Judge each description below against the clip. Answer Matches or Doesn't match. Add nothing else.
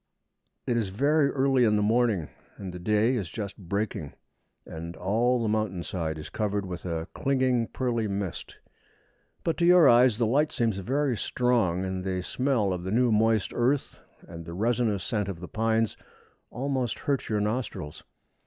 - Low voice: Matches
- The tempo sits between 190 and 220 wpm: Doesn't match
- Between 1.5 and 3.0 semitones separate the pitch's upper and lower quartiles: Doesn't match